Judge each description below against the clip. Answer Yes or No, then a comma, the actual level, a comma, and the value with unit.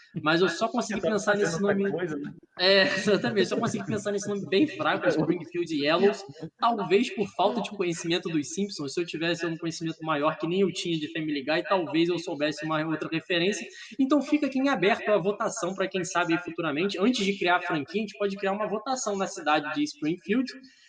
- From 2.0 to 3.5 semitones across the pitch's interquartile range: No, average, 4.0 semitones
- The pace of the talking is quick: Yes, fast, 200 wpm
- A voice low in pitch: No, high, 190 Hz